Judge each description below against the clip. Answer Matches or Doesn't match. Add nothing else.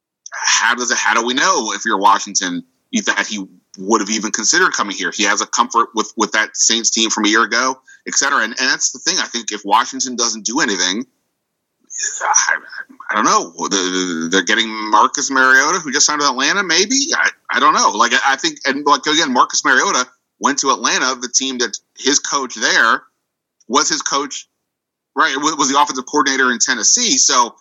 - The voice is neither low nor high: Doesn't match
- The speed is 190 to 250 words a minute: Matches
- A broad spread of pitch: Matches